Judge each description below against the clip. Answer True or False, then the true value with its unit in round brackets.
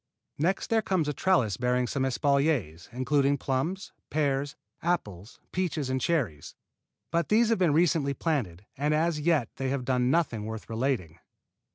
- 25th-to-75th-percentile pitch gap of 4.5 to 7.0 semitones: True (5.0 semitones)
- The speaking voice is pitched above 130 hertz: True (140 Hz)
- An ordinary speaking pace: True (155 wpm)